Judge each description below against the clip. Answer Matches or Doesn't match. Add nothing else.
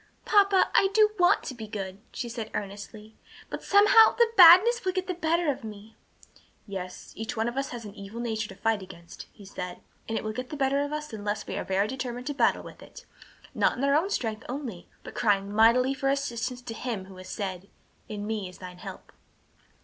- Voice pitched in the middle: Doesn't match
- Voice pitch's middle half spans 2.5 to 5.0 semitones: Doesn't match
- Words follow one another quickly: Matches